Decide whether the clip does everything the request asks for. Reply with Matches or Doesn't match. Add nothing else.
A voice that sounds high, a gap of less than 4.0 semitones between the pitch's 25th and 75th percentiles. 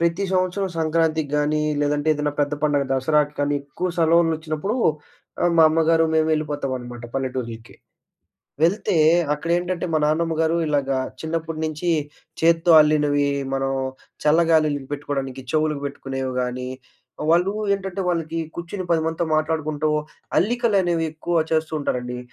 Doesn't match